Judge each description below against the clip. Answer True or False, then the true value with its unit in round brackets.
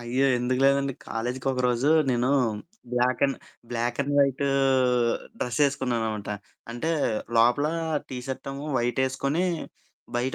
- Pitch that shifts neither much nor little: False (2.2 semitones)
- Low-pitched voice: True (130 Hz)